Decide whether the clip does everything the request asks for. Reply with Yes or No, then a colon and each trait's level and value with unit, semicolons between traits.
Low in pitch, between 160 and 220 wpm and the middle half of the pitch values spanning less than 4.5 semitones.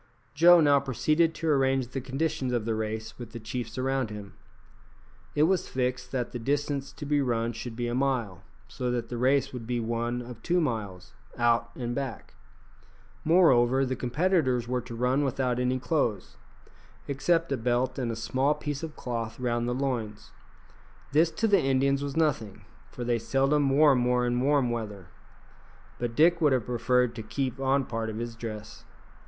Yes: low, 125 Hz; average, 180 wpm; average, 3.0 semitones